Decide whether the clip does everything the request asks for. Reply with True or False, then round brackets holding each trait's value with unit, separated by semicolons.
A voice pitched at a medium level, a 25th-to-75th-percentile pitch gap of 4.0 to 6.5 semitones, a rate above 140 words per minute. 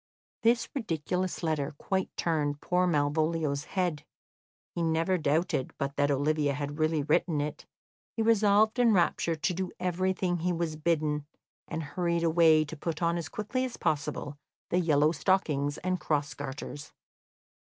False (160 Hz; 3.6 semitones; 150 wpm)